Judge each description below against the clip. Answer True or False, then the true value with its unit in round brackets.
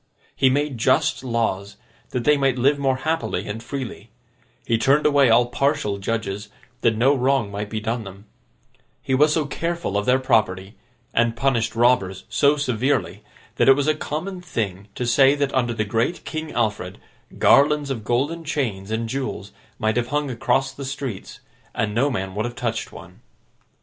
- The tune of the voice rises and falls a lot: False (4.4 semitones)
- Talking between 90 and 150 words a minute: False (175 wpm)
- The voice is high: False (125 Hz)